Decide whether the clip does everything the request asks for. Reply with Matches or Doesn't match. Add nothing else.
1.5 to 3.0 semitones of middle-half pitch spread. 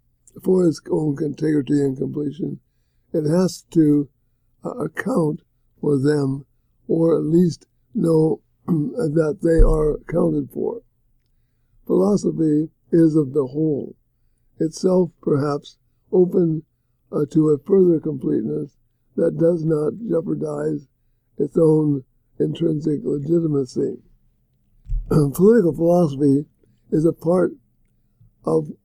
Doesn't match